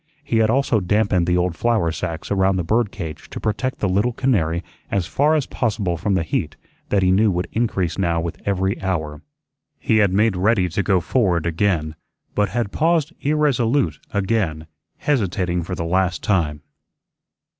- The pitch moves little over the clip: No, average, 4.5 semitones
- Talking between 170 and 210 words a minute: Yes, average, 175 wpm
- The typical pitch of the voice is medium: No, very low, 95 Hz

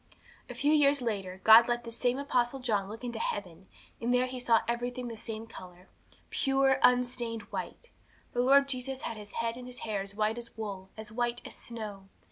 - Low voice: No, high, 235 Hz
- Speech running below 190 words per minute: No, average, 200 wpm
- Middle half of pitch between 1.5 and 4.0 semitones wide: Yes, average, 2.7 semitones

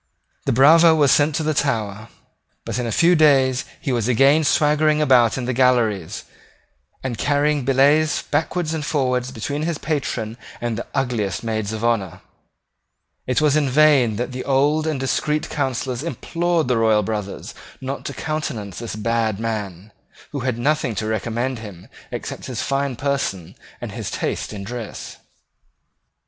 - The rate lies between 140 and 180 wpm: Yes, average, 155 wpm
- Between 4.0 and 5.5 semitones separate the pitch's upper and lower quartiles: Yes, average, 4.8 semitones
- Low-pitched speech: Yes, low, 130 Hz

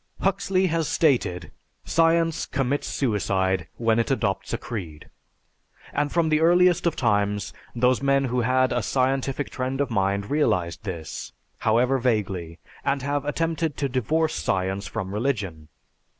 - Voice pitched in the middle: No, low, 125 Hz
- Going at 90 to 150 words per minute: Yes, average, 140 wpm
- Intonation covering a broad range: Yes, wide, 6.5 semitones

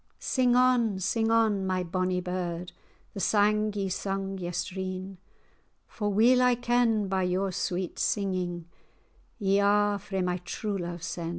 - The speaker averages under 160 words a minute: Yes, average, 140 wpm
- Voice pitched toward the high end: Yes, high, 195 Hz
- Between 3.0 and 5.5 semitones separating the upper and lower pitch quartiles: No, narrow, 2.6 semitones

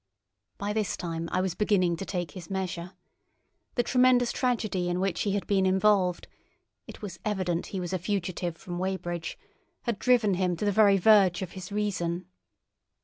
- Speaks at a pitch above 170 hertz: Yes, high, 190 Hz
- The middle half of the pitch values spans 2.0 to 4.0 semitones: Yes, average, 2.9 semitones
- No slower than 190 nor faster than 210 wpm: No, average, 165 wpm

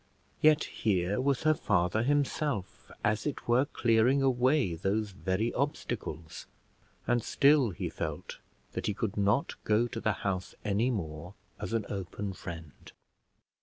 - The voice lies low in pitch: Yes, low, 110 Hz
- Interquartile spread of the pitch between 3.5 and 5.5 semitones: Yes, average, 5.0 semitones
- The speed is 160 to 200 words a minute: No, average, 140 wpm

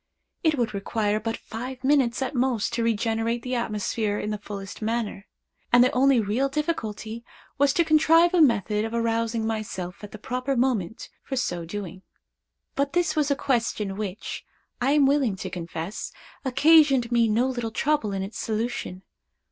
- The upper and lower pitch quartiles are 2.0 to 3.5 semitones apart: No, average, 4.1 semitones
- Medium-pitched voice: No, high, 230 Hz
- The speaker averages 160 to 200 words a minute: Yes, average, 170 wpm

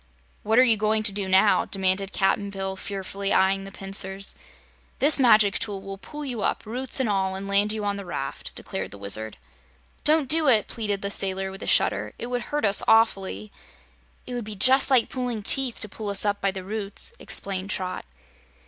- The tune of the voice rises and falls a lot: No, average, 2.9 semitones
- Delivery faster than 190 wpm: Yes, average, 200 wpm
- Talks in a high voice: Yes, high, 200 Hz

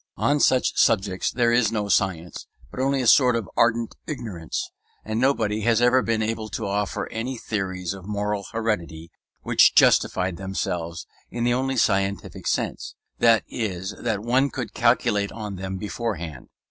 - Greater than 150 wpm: Yes, average, 160 wpm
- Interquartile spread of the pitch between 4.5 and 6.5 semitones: No, average, 3.6 semitones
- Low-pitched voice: Yes, low, 105 Hz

